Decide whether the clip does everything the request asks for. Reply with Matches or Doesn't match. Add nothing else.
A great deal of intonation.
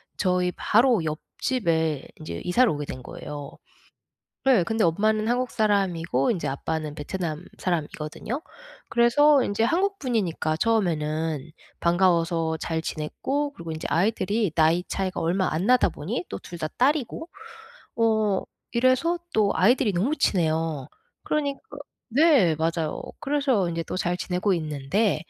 Matches